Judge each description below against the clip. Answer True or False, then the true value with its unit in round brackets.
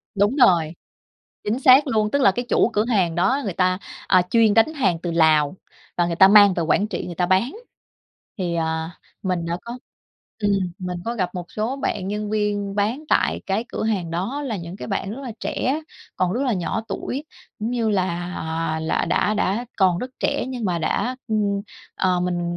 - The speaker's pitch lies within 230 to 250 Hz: False (200 Hz)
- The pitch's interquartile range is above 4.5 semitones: False (4.2 semitones)